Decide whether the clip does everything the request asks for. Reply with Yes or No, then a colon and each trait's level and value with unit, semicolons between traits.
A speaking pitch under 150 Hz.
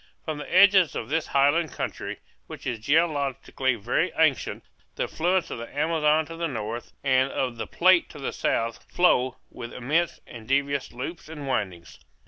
Yes: medium, 140 Hz